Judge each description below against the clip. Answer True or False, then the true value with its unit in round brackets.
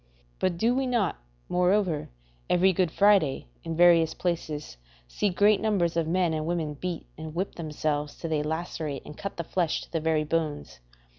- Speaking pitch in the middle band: True (170 Hz)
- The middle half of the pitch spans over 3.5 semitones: False (3.1 semitones)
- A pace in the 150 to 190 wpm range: True (175 wpm)